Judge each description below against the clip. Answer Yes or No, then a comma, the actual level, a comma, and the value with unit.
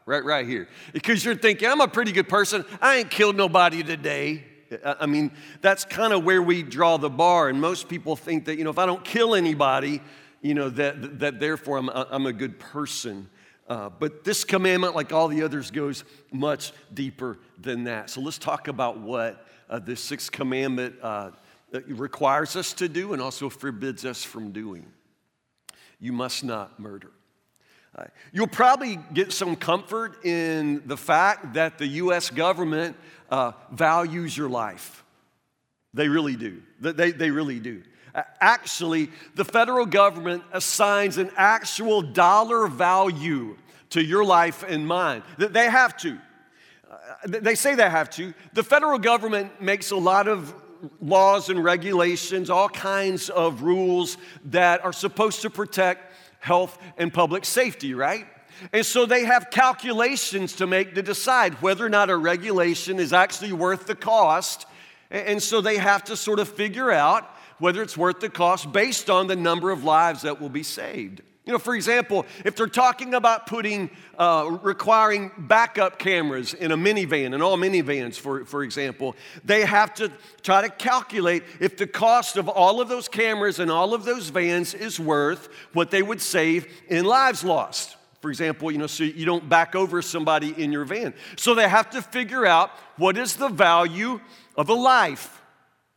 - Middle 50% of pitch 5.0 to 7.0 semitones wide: Yes, wide, 5.4 semitones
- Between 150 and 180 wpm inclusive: Yes, average, 170 wpm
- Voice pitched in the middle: Yes, medium, 175 Hz